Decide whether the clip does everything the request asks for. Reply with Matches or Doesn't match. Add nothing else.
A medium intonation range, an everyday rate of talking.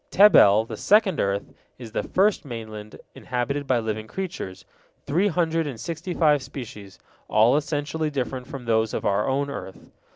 Doesn't match